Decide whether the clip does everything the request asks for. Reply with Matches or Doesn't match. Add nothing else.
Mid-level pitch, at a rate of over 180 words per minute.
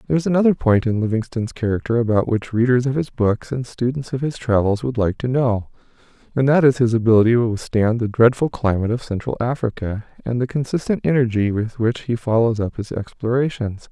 Doesn't match